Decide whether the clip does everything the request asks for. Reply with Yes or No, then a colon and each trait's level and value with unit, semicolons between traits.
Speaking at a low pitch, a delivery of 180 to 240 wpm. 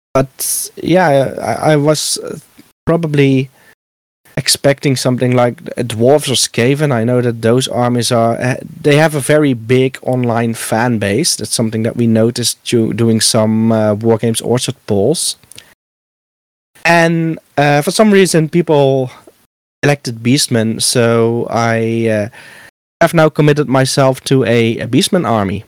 No: low, 125 Hz; slow, 135 wpm